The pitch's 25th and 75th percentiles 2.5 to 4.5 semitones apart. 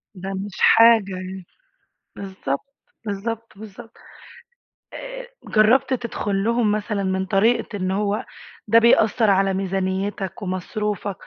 Yes: average, 2.9 semitones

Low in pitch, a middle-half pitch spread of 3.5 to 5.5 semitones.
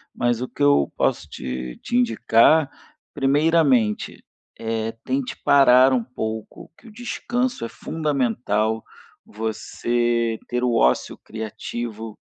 Yes: low, 120 Hz; average, 4.4 semitones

